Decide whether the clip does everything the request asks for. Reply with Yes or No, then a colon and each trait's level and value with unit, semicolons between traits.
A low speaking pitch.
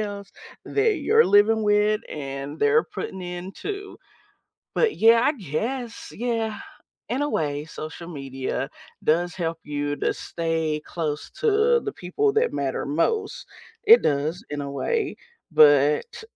No: medium, 180 Hz